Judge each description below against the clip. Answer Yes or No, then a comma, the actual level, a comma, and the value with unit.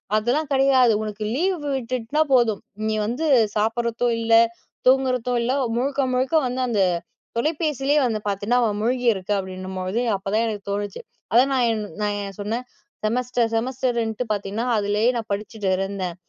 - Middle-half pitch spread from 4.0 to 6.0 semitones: No, average, 3.4 semitones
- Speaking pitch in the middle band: No, high, 230 Hz